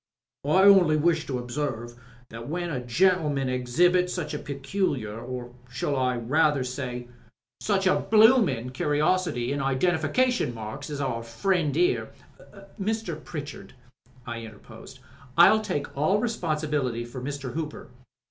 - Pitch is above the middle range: No, medium, 145 Hz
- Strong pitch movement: Yes, wide, 6.1 semitones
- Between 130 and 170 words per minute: Yes, average, 140 wpm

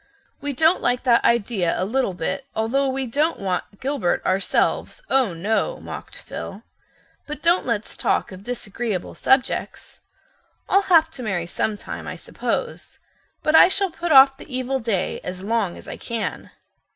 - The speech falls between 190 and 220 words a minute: No, average, 160 wpm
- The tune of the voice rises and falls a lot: Yes, wide, 5.7 semitones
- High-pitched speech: Yes, high, 245 Hz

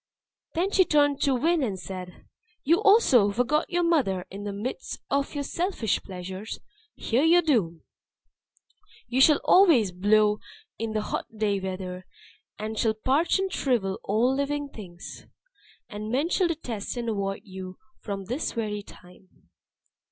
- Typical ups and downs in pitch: No, wide, 6.8 semitones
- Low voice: No, high, 225 Hz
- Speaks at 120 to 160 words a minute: Yes, average, 150 wpm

